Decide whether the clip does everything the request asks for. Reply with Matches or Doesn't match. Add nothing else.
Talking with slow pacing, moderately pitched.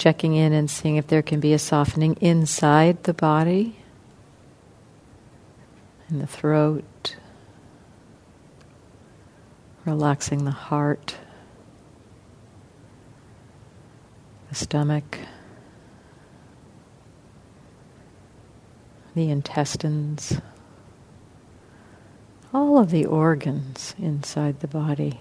Matches